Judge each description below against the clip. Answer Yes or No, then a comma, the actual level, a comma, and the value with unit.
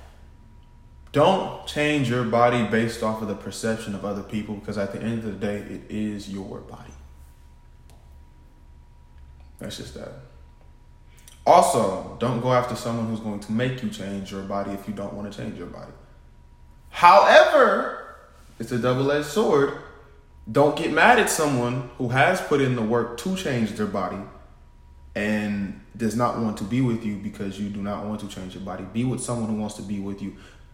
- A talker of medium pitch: No, low, 105 Hz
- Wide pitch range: Yes, wide, 8.8 semitones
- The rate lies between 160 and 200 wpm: Yes, average, 185 wpm